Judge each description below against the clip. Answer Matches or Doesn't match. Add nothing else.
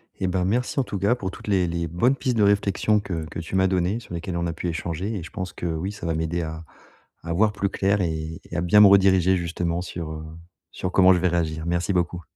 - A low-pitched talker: Matches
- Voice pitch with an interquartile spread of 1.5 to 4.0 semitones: Matches